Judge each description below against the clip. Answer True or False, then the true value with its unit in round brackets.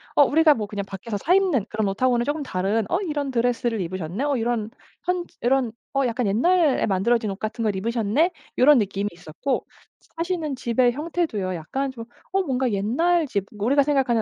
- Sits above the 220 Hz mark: True (240 Hz)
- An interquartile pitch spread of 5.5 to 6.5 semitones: True (5.8 semitones)